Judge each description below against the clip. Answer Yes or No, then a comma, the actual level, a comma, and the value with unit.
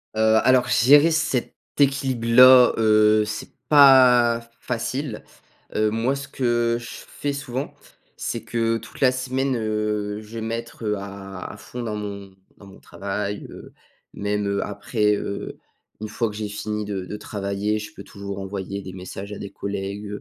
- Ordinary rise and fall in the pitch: Yes, average, 3.0 semitones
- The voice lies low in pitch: Yes, low, 110 Hz